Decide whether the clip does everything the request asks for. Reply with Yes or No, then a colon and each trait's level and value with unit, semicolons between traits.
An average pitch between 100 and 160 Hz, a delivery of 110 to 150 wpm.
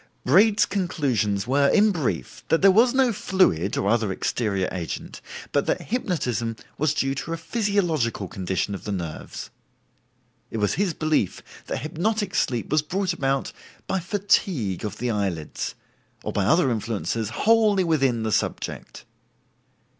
Yes: medium, 140 Hz; average, 145 wpm